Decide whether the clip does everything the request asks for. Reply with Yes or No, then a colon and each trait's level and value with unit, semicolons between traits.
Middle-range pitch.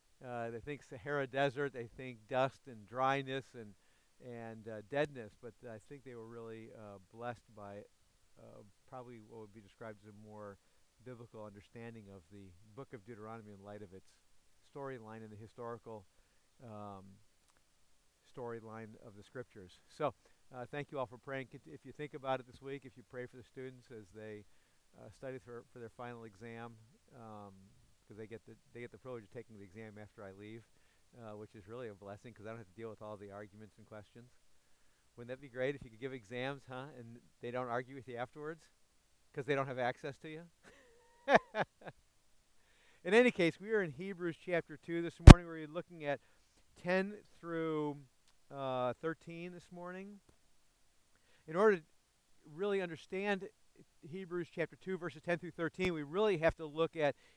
No: low, 120 Hz